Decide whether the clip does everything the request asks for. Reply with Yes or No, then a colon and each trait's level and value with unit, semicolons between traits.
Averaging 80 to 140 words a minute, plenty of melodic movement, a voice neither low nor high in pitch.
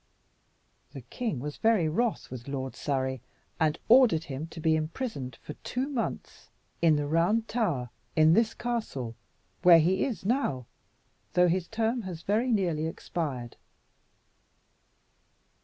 Yes: slow, 135 wpm; wide, 7.5 semitones; medium, 165 Hz